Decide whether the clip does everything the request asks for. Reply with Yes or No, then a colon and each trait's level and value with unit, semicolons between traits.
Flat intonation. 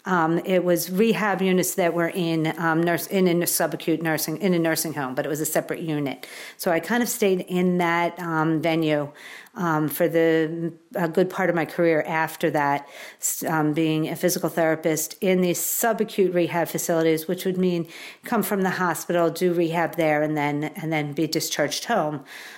Yes: narrow, 2.1 semitones